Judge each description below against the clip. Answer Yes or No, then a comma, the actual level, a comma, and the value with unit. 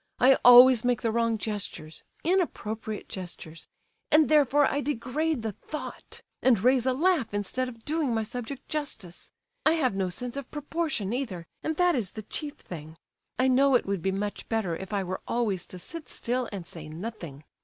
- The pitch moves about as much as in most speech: No, wide, 6.1 semitones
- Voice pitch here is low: No, high, 235 Hz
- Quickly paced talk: No, average, 175 wpm